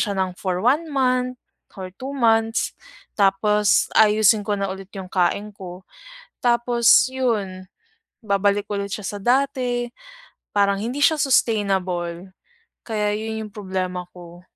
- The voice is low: No, high, 210 Hz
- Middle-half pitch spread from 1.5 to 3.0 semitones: No, average, 3.9 semitones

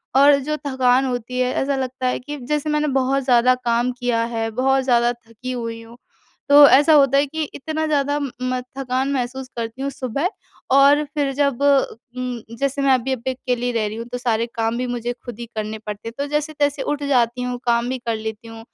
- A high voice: Yes, very high, 255 Hz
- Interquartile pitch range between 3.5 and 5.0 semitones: No, average, 2.8 semitones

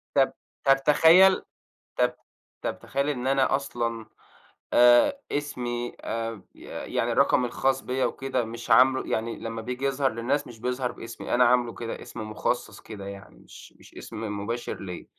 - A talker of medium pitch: No, low, 120 Hz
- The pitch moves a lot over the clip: No, average, 2.8 semitones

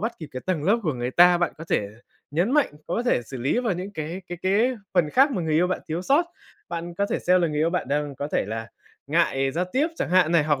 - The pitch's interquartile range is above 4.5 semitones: No, average, 4.2 semitones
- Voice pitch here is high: No, medium, 170 Hz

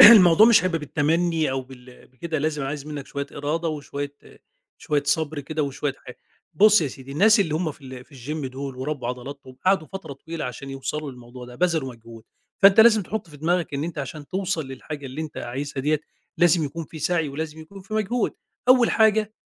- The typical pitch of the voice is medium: Yes, medium, 150 Hz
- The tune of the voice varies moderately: Yes, average, 4.1 semitones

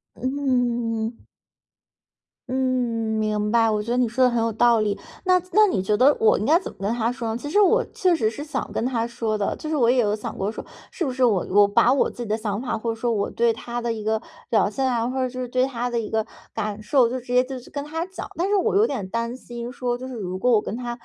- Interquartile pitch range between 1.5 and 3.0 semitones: Yes, average, 2.7 semitones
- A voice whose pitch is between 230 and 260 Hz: Yes, high, 235 Hz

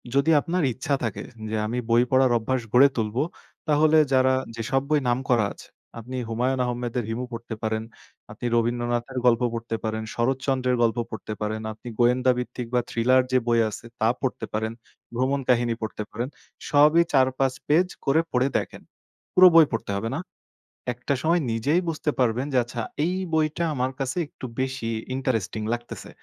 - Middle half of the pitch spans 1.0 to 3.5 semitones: Yes, narrow, 2.6 semitones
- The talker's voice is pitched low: Yes, low, 125 Hz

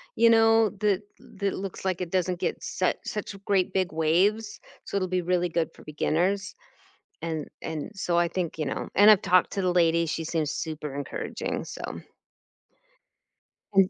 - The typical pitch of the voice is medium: Yes, medium, 180 Hz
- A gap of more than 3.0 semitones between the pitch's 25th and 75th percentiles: Yes, average, 3.4 semitones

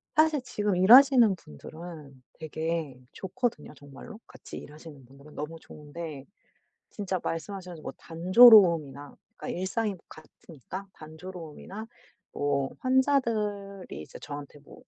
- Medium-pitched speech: Yes, medium, 170 Hz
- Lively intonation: Yes, wide, 5.7 semitones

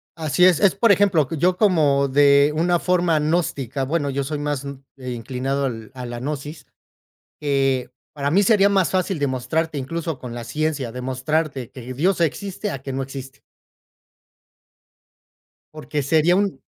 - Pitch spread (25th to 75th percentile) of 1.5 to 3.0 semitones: No, average, 4.1 semitones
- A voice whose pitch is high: No, medium, 145 Hz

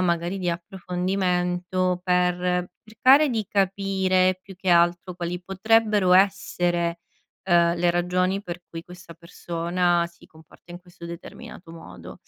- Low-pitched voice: No, medium, 180 Hz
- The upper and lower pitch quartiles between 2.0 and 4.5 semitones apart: No, narrow, 1.4 semitones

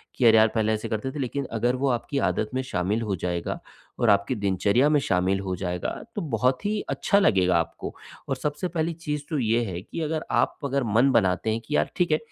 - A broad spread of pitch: Yes, wide, 6.6 semitones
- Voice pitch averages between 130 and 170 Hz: No, low, 115 Hz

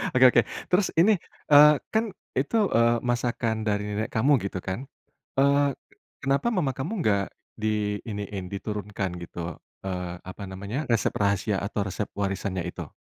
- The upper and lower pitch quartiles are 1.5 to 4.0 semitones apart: No, average, 5.1 semitones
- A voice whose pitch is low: Yes, low, 105 Hz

